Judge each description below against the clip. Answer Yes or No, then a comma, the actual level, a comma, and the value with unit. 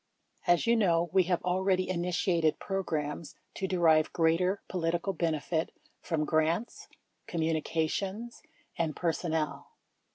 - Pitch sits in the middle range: Yes, medium, 170 Hz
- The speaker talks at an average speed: No, slow, 130 wpm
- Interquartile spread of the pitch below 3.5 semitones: Yes, narrow, 2.6 semitones